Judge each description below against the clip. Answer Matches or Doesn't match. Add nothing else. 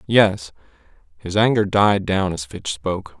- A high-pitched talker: Doesn't match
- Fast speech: Doesn't match